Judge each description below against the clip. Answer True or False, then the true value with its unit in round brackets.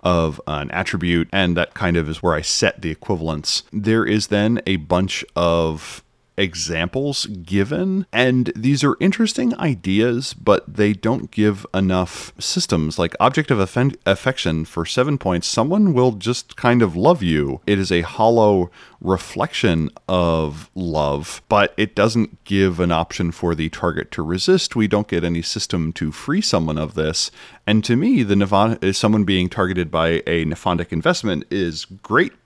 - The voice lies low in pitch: True (95 Hz)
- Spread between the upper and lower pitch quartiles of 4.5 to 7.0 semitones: True (5.1 semitones)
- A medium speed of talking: True (165 wpm)